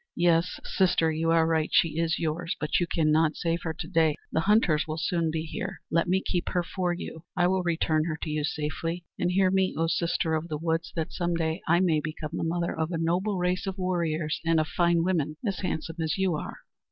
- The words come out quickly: Yes, fast, 230 wpm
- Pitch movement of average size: No, narrow, 1.8 semitones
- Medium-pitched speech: Yes, medium, 165 Hz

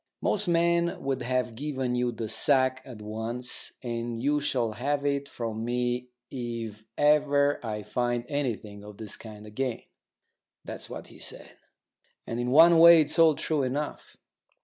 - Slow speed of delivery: No, average, 155 wpm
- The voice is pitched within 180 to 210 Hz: No, low, 125 Hz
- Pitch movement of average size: Yes, average, 3.8 semitones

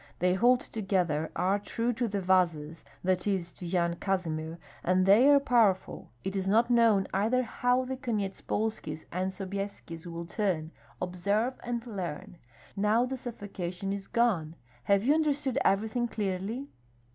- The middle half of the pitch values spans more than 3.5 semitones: Yes, average, 4.5 semitones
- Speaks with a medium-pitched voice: No, high, 195 Hz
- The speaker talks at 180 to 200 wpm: No, average, 145 wpm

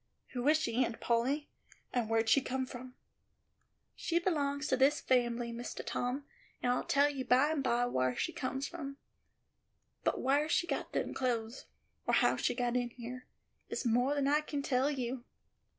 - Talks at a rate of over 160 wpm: Yes, average, 180 wpm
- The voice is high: Yes, very high, 255 Hz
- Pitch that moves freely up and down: No, average, 2.8 semitones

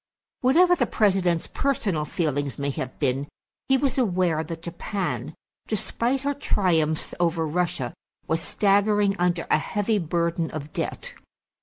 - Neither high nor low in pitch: Yes, medium, 175 Hz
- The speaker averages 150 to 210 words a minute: No, slow, 135 wpm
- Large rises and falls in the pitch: No, average, 4.9 semitones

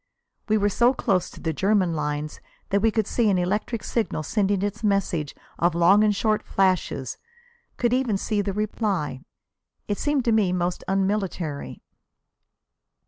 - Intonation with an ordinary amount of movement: Yes, average, 3.4 semitones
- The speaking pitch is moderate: No, high, 200 Hz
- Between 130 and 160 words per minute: Yes, average, 155 wpm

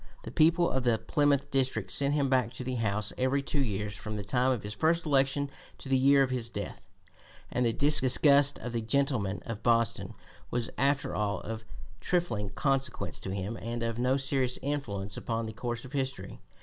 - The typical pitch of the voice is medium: No, low, 125 Hz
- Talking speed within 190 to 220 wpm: Yes, average, 195 wpm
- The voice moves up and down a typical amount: Yes, average, 3.7 semitones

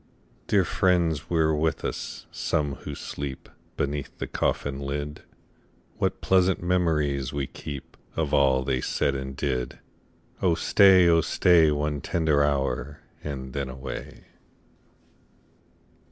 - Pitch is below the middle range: Yes, very low, 75 Hz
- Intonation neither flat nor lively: Yes, average, 3.1 semitones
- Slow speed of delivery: Yes, slow, 125 wpm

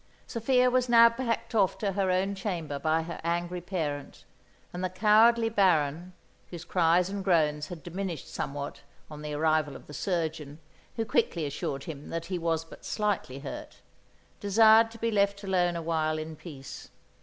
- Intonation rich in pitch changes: No, average, 4.4 semitones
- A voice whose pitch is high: No, medium, 175 Hz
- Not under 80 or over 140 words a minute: No, average, 170 wpm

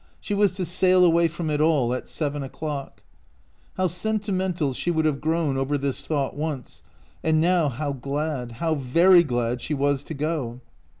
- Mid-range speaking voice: Yes, medium, 155 Hz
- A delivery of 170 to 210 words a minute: Yes, average, 180 wpm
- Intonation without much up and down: No, average, 3.8 semitones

